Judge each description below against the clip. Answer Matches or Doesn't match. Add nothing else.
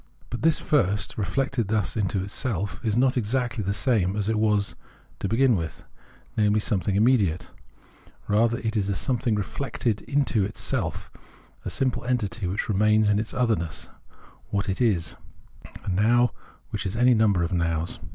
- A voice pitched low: Matches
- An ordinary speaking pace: Matches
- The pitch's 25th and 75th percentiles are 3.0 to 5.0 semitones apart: Matches